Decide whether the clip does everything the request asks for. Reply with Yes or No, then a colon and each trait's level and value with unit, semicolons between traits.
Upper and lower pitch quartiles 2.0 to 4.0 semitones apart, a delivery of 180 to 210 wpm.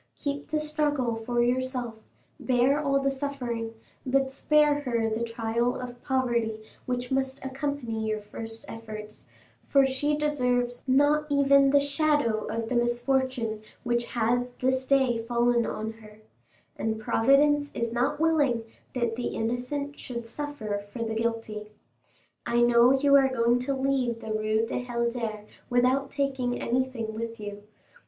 No: average, 3.2 semitones; average, 145 wpm